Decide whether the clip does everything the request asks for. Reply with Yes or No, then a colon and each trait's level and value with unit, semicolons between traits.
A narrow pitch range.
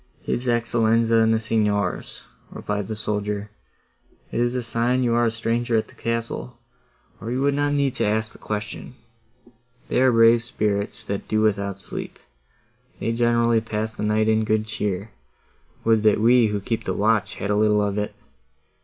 Yes: narrow, 2.0 semitones